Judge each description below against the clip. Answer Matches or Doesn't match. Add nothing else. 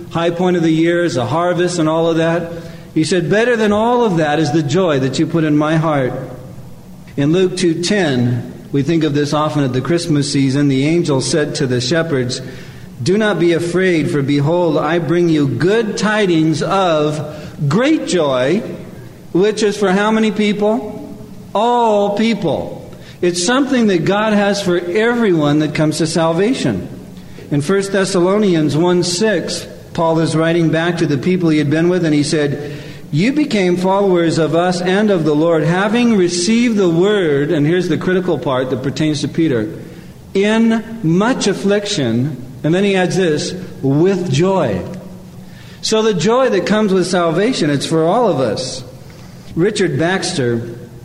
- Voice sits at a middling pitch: Matches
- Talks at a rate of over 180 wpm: Doesn't match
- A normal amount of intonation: Matches